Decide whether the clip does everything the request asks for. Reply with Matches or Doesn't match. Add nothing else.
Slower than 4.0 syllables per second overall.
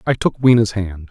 Doesn't match